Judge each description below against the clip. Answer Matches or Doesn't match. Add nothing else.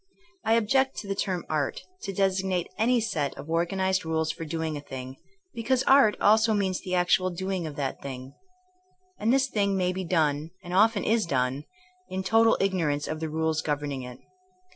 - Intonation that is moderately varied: Matches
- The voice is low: Doesn't match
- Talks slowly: Doesn't match